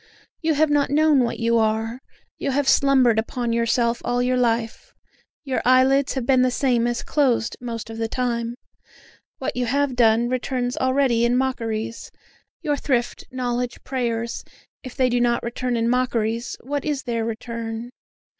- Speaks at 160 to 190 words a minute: Yes, average, 165 wpm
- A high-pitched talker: Yes, high, 245 Hz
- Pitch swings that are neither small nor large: No, narrow, 2.0 semitones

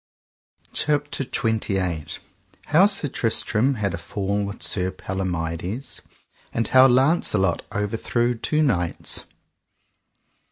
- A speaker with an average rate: No, slow, 95 wpm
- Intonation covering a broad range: Yes, wide, 5.7 semitones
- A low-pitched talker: Yes, low, 110 Hz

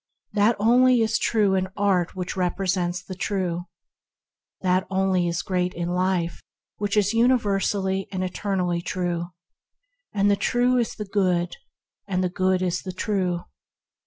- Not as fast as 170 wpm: Yes, average, 140 wpm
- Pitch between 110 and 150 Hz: No, high, 190 Hz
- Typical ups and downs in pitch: No, narrow, 2.2 semitones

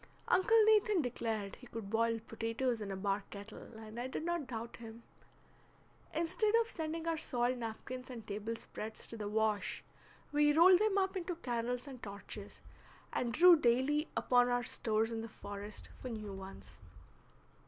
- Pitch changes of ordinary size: No, wide, 5.8 semitones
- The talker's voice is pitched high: Yes, high, 240 Hz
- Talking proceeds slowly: No, average, 165 wpm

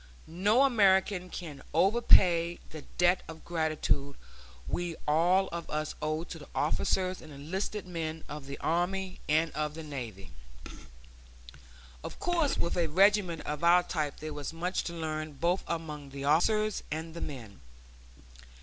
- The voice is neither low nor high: Yes, medium, 165 Hz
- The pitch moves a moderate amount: Yes, average, 3.2 semitones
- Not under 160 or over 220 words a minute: No, average, 150 wpm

